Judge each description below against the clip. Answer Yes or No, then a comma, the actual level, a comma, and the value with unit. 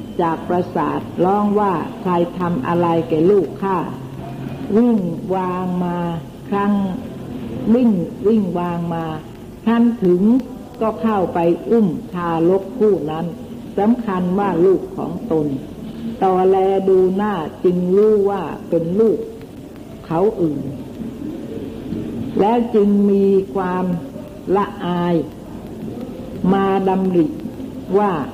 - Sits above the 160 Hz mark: Yes, high, 190 Hz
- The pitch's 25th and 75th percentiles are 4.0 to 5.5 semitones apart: No, average, 3.2 semitones